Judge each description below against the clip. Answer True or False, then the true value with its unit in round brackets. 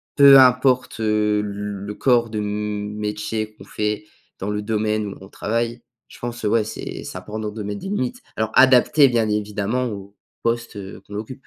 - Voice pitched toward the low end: True (105 Hz)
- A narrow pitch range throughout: True (2.3 semitones)